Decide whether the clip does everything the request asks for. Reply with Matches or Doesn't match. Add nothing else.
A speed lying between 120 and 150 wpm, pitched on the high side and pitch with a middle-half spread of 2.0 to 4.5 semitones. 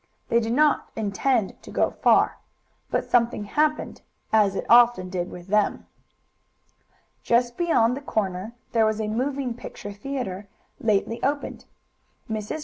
Matches